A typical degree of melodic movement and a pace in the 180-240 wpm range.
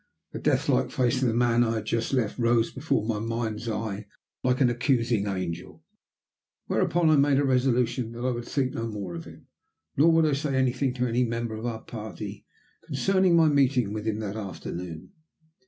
Yes: average, 3.2 semitones; average, 195 wpm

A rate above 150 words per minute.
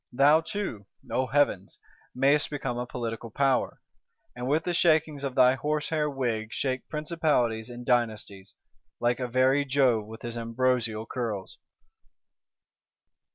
No: slow, 135 wpm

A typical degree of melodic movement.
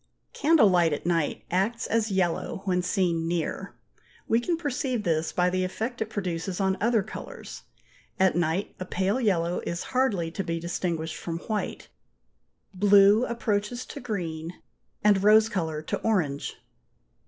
Yes: average, 4.2 semitones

